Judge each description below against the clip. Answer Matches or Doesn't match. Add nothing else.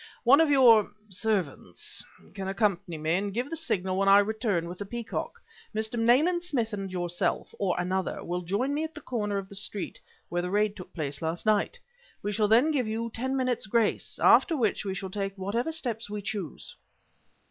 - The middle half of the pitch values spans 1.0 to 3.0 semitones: Doesn't match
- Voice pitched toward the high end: Matches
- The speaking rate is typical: Matches